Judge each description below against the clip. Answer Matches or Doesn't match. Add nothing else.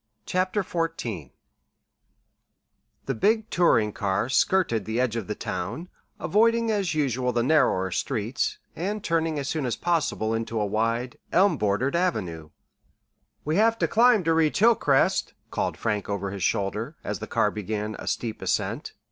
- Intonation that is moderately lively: Doesn't match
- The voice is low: Matches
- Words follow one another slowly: Doesn't match